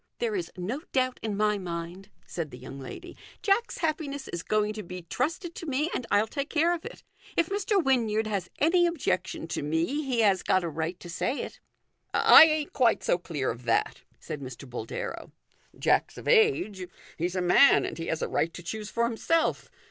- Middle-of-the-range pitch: No, high, 215 Hz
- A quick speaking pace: Yes, fast, 210 wpm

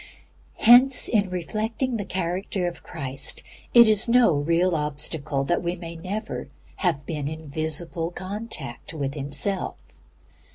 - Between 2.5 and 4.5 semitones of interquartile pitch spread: No, average, 5.3 semitones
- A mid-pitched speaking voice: Yes, medium, 175 Hz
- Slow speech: Yes, slow, 130 wpm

